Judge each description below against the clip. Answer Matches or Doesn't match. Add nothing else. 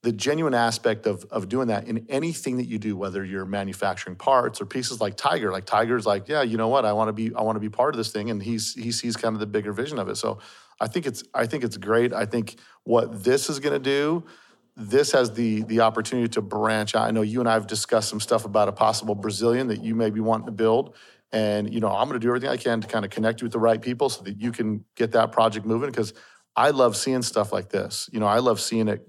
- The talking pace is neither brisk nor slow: Doesn't match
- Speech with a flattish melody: Matches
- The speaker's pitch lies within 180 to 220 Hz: Doesn't match